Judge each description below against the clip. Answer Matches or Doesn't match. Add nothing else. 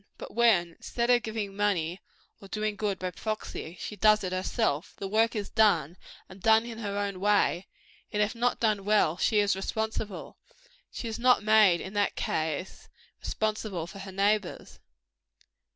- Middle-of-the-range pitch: Doesn't match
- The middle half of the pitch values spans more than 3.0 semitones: Doesn't match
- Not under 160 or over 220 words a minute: Matches